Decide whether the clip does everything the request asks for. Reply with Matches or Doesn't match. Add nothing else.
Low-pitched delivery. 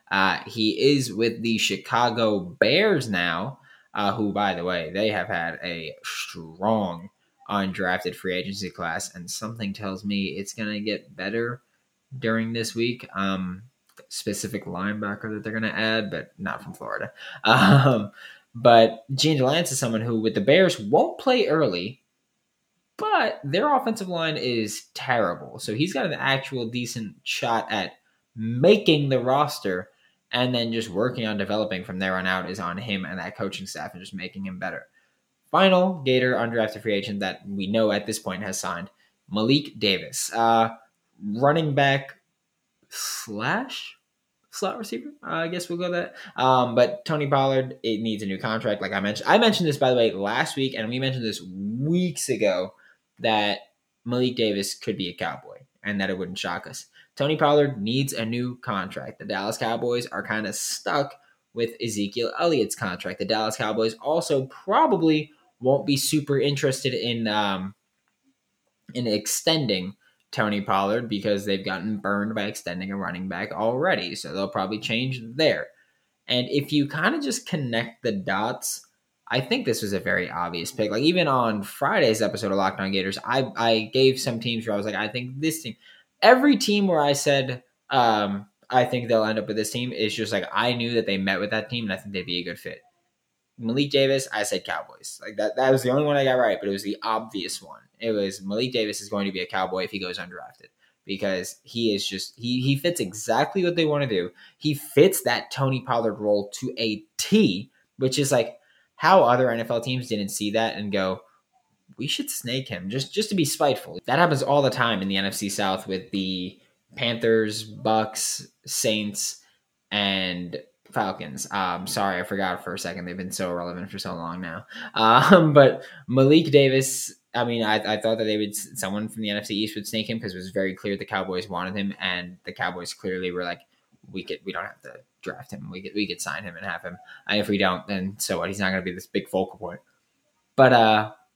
Matches